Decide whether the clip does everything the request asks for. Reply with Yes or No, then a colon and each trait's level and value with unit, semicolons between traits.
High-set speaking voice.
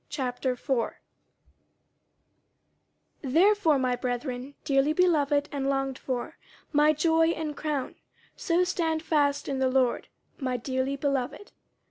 Yes: very high, 280 Hz